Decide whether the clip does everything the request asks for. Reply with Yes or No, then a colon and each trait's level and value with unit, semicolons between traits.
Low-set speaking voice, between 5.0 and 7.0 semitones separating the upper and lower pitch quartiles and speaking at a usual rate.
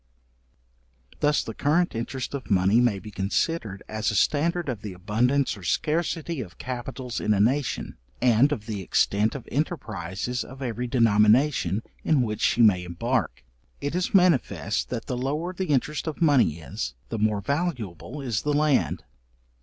Yes: low, 125 Hz; wide, 5.5 semitones; average, 160 wpm